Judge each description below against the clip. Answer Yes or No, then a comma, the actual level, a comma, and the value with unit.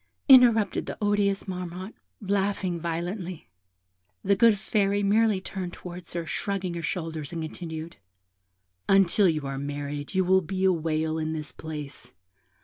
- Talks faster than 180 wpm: No, average, 145 wpm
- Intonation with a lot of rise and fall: No, average, 3.8 semitones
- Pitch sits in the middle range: Yes, medium, 180 Hz